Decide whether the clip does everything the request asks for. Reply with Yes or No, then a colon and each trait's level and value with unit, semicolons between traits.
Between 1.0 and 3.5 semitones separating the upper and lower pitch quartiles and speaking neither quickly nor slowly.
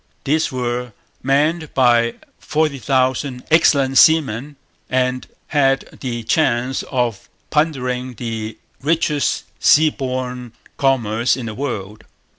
No: average, 3.1 semitones; slow, 105 wpm